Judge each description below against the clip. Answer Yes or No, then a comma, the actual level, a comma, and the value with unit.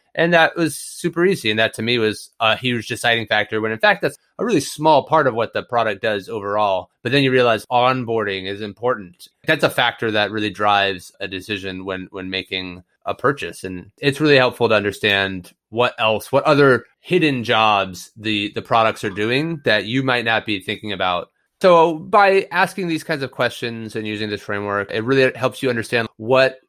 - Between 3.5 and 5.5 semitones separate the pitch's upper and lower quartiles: Yes, average, 4.2 semitones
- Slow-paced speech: No, average, 200 wpm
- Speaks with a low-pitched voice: Yes, low, 115 Hz